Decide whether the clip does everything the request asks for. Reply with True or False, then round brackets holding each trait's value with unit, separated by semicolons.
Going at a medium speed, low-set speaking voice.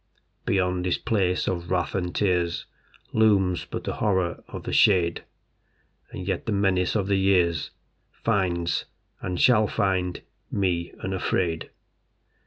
False (130 wpm; 90 Hz)